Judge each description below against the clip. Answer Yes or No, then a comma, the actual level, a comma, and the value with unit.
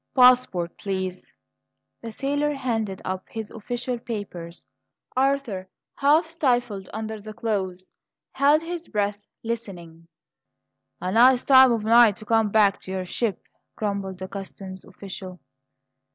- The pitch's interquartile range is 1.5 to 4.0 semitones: No, average, 4.7 semitones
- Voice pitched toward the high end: Yes, high, 215 Hz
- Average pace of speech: No, slow, 125 wpm